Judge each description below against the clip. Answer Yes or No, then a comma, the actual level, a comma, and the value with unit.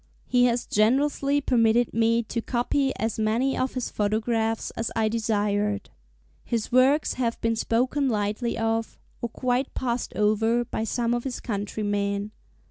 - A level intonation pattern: Yes, narrow, 2.3 semitones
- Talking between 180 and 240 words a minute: No, average, 145 wpm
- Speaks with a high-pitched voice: Yes, high, 230 Hz